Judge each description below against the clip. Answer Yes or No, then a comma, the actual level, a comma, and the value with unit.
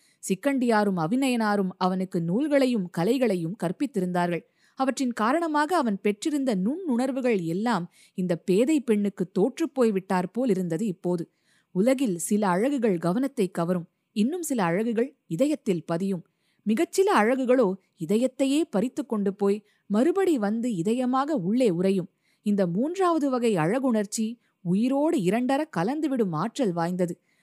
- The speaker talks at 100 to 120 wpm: Yes, average, 110 wpm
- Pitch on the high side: Yes, high, 220 Hz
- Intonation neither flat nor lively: No, wide, 6.0 semitones